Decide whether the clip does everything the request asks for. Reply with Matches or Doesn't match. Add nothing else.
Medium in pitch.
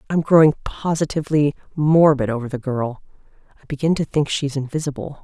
Matches